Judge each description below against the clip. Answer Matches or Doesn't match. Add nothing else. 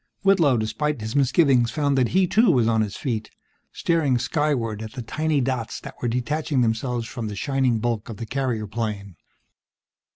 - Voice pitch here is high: Doesn't match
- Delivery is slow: Doesn't match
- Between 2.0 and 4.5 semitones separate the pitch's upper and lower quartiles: Matches